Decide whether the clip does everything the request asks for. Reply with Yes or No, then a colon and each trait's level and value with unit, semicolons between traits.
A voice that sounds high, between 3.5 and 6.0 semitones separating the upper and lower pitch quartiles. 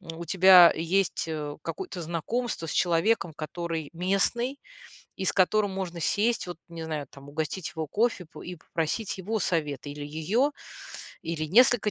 No: medium, 175 Hz; average, 4.0 semitones